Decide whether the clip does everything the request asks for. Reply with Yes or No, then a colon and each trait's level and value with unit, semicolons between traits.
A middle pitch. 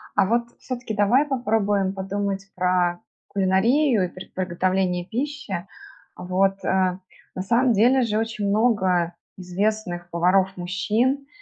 No: high, 195 Hz